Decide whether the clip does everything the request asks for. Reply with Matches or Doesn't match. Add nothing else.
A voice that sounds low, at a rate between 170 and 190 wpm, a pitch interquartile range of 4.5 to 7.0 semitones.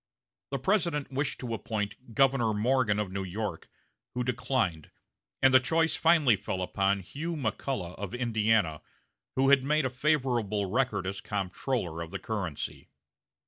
Doesn't match